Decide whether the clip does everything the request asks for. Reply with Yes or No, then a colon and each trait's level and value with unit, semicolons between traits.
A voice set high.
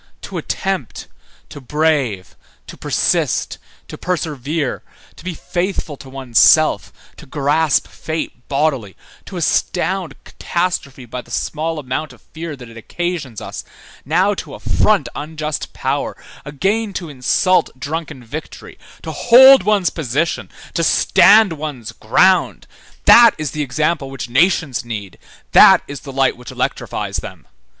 No: medium, 155 Hz